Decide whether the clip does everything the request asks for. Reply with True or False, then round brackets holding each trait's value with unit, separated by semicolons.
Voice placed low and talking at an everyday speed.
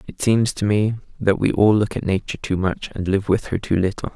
False (100 Hz; 260 wpm)